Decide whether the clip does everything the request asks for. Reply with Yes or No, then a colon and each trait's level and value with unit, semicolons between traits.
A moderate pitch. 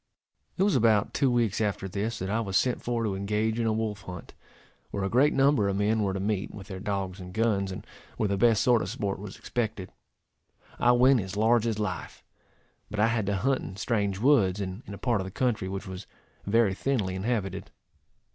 No: low, 105 Hz